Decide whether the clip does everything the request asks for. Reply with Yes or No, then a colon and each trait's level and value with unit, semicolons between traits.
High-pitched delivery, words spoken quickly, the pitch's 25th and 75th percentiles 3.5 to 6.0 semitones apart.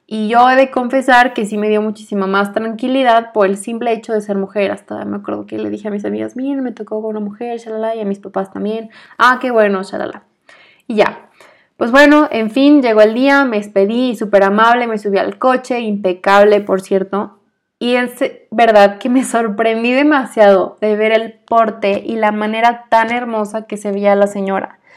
No: high, 220 Hz; fast, 205 wpm; average, 3.0 semitones